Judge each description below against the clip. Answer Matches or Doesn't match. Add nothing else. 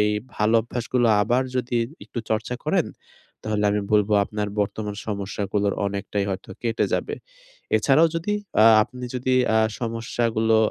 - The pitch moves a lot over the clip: Doesn't match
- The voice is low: Matches